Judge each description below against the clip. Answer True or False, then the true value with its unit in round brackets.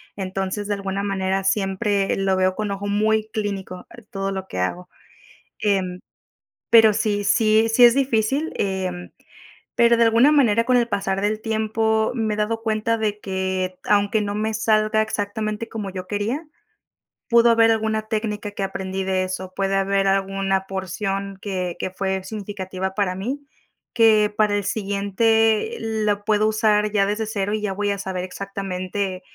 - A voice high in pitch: True (205 Hz)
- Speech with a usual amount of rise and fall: False (2.2 semitones)